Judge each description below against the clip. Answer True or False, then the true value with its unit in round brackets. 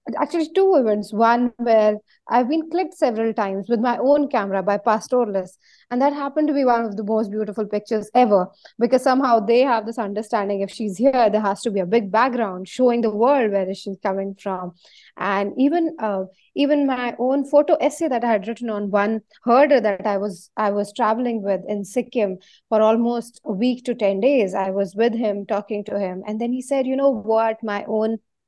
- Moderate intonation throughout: True (3.4 semitones)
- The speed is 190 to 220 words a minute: True (205 wpm)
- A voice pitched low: False (225 Hz)